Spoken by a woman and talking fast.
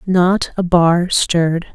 No: female; slow, 135 wpm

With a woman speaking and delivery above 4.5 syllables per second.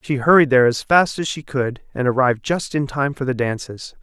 No: male; 5.5 syllables/s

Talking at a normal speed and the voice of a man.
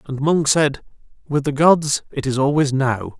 Yes: average, 190 wpm; male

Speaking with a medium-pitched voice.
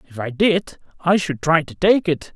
Yes: medium, 165 Hz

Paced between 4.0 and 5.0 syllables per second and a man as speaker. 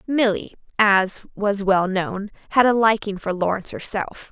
No: 4.4 syllables/s; female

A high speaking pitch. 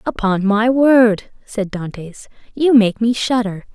Yes: high, 220 Hz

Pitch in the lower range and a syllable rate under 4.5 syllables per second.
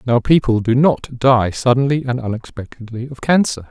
No: low, 125 Hz; 5.0 syllables/s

